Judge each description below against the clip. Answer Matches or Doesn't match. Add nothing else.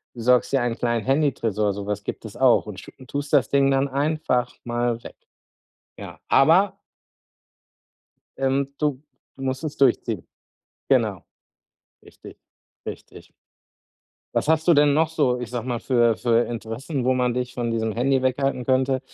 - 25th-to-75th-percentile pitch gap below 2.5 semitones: Doesn't match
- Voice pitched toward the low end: Matches